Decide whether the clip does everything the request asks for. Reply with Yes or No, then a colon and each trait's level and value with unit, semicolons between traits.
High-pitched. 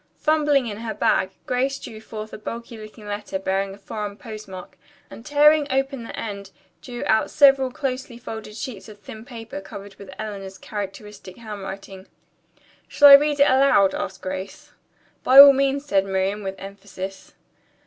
Yes: high, 215 Hz